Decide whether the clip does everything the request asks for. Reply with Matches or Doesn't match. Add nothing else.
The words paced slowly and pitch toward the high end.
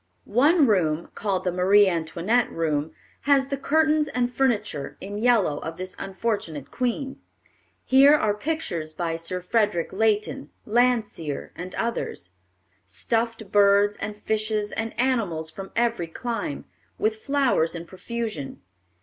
Matches